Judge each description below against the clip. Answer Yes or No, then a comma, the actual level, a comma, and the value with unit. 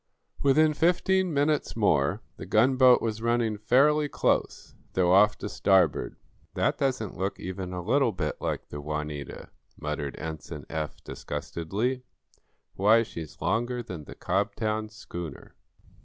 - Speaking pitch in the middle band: No, low, 105 Hz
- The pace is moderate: No, slow, 130 wpm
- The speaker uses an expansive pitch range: Yes, wide, 7.0 semitones